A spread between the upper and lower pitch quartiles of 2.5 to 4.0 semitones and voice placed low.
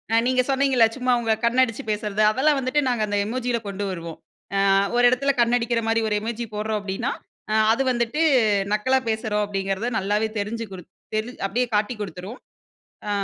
No: average, 3.1 semitones; high, 225 Hz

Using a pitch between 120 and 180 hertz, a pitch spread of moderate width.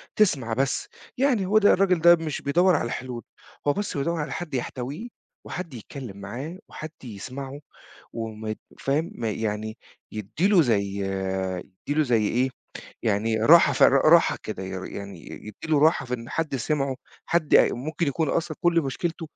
No: medium, 140 Hz; wide, 6.7 semitones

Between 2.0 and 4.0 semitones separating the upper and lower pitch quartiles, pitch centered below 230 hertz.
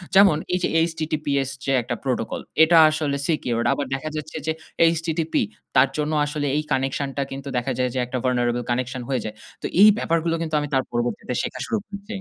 Yes: average, 3.7 semitones; medium, 140 Hz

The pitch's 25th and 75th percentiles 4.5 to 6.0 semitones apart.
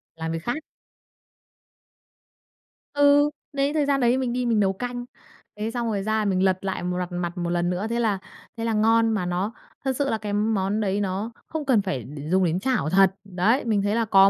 No: average, 4.1 semitones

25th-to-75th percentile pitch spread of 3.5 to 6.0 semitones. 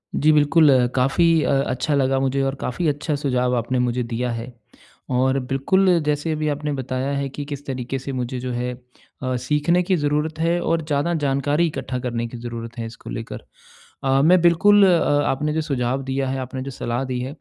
No: average, 3.1 semitones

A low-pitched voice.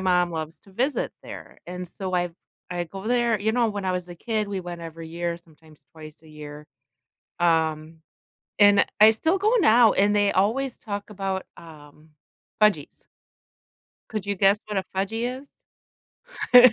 No: high, 190 Hz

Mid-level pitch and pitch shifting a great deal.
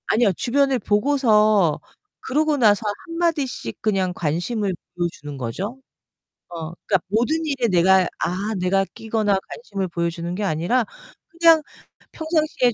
No: high, 210 Hz; wide, 6.5 semitones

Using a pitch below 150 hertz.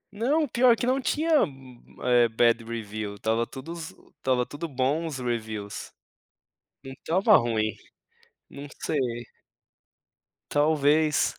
Yes: low, 135 Hz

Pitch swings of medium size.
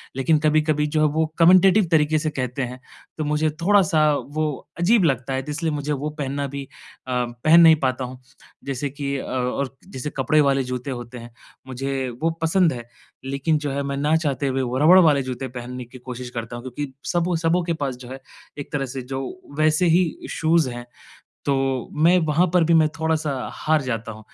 Yes: average, 3.5 semitones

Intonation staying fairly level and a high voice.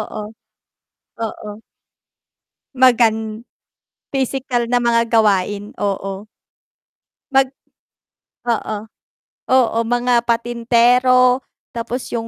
Yes: narrow, 2.3 semitones; high, 235 Hz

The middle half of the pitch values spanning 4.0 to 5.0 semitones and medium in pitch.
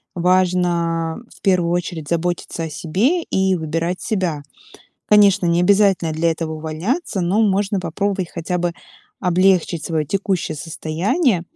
No: average, 2.8 semitones; medium, 175 Hz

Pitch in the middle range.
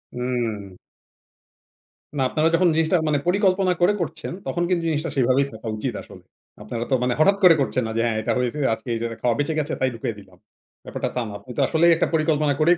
Yes: medium, 145 Hz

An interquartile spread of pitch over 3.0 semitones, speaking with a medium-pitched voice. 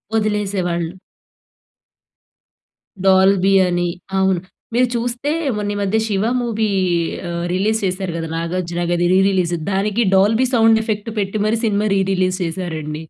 No: average, 3.4 semitones; high, 195 Hz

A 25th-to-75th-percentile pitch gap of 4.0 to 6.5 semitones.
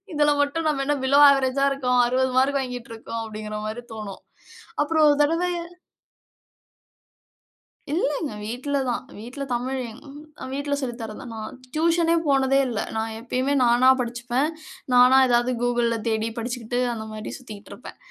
No: average, 3.3 semitones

